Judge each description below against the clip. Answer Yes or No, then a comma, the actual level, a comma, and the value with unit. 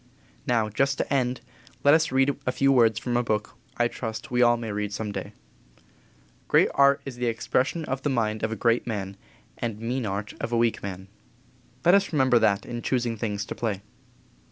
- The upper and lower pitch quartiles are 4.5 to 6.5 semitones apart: No, average, 3.3 semitones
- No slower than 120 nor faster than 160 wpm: No, fast, 205 wpm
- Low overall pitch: Yes, low, 120 Hz